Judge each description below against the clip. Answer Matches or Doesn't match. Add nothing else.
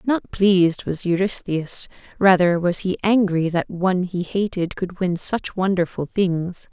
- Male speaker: Doesn't match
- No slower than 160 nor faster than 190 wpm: Doesn't match